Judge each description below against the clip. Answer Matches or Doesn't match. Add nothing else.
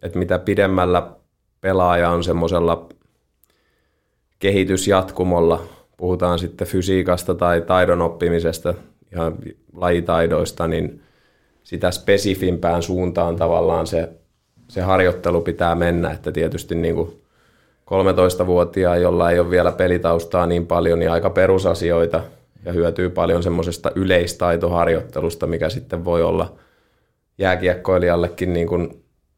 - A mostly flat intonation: Matches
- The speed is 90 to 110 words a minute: Matches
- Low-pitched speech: Matches